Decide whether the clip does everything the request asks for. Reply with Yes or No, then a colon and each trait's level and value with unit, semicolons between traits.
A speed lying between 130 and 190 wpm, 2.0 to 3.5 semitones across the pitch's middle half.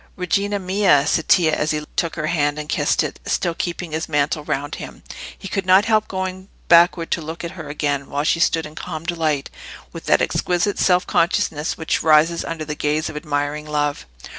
No: average, 200 wpm; average, 2.9 semitones